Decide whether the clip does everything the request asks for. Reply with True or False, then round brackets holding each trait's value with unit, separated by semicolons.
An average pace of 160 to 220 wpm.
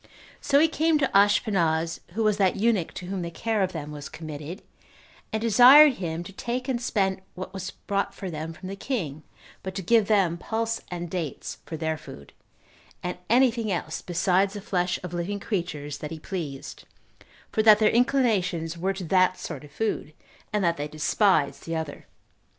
True (190 wpm)